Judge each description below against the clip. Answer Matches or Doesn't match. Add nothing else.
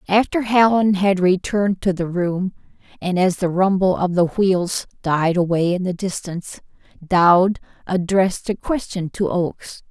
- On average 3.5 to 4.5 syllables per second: Matches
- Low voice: Doesn't match